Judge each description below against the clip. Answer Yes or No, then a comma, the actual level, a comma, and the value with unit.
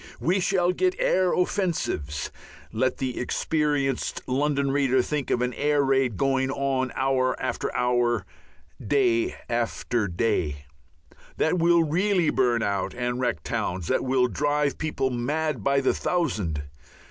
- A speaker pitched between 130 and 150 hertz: Yes, low, 135 Hz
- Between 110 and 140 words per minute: Yes, slow, 135 wpm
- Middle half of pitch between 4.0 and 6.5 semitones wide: Yes, average, 4.4 semitones